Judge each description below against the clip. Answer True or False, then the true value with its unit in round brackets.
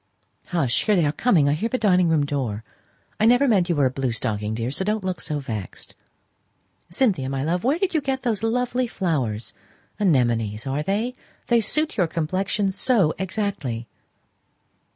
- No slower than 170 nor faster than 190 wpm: True (175 wpm)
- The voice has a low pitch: False (175 Hz)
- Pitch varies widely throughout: True (8.4 semitones)